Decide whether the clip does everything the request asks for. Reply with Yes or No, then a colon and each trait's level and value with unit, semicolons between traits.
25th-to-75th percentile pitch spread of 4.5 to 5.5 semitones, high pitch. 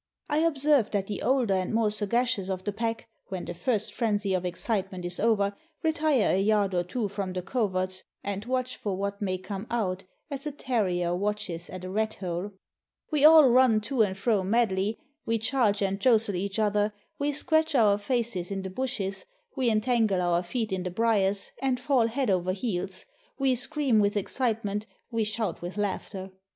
No: average, 4.1 semitones; high, 210 Hz